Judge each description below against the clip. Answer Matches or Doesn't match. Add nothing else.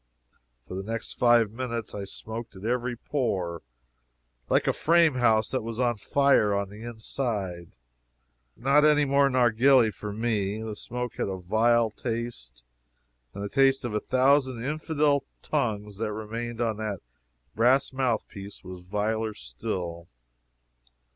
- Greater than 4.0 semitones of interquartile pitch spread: Doesn't match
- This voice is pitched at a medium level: Doesn't match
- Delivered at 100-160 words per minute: Matches